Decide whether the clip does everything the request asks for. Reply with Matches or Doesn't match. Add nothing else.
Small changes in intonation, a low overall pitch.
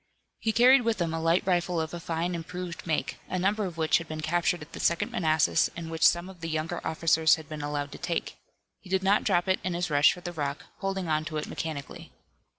Doesn't match